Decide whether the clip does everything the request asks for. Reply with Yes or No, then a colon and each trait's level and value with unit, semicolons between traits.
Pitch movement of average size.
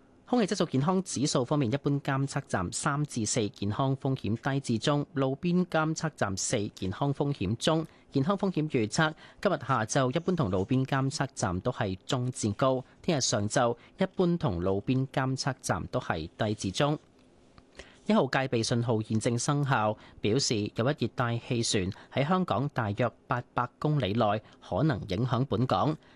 Yes: average, 4.7 semitones